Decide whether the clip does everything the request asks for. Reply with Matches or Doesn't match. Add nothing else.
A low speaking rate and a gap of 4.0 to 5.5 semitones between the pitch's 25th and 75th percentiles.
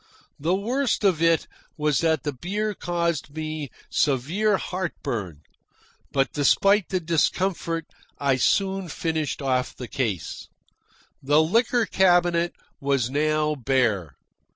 Matches